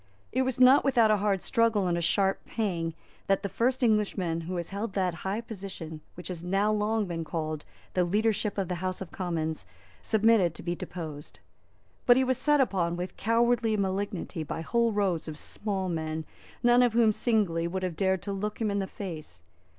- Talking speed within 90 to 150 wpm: No, average, 195 wpm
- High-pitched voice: Yes, high, 195 Hz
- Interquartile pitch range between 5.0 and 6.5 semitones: No, average, 4.3 semitones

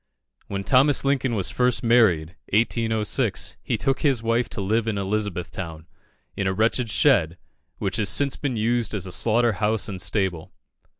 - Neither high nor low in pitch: No, low, 110 Hz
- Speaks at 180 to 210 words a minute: No, average, 165 wpm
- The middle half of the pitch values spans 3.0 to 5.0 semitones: Yes, average, 3.8 semitones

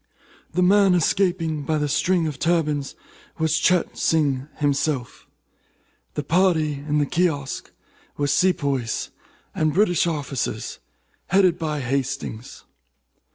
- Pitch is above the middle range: No, medium, 155 Hz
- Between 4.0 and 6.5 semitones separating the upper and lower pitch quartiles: No, average, 3.6 semitones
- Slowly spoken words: Yes, slow, 110 wpm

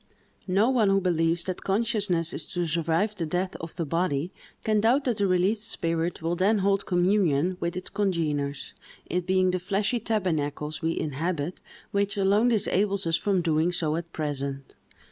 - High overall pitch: No, medium, 180 Hz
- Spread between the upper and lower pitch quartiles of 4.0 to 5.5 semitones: No, average, 3.4 semitones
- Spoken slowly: No, average, 170 wpm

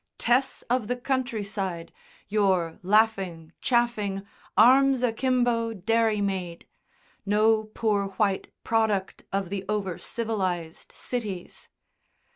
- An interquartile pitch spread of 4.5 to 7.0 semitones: No, average, 3.2 semitones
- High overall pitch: Yes, high, 210 Hz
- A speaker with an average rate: No, slow, 90 wpm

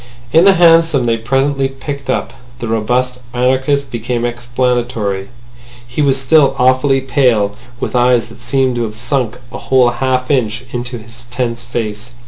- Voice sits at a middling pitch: No, low, 125 Hz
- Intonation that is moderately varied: No, narrow, 2.1 semitones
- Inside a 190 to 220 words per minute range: No, average, 155 wpm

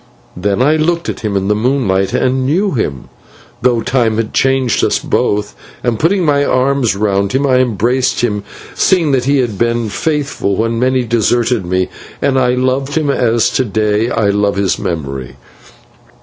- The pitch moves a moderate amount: Yes, average, 4.4 semitones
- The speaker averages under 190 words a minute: Yes, average, 175 wpm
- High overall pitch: No, low, 120 Hz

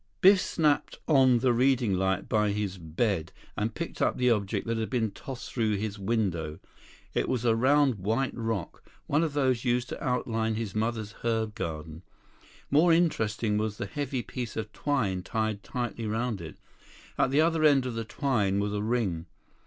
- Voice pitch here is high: No, low, 115 Hz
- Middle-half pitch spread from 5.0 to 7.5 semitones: No, average, 3.9 semitones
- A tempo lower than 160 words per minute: No, average, 180 wpm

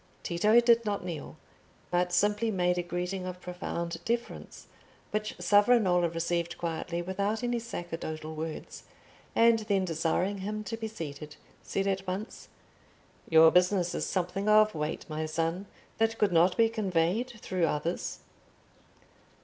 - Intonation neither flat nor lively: Yes, average, 3.9 semitones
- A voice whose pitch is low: No, medium, 185 Hz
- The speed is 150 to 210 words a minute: No, average, 140 wpm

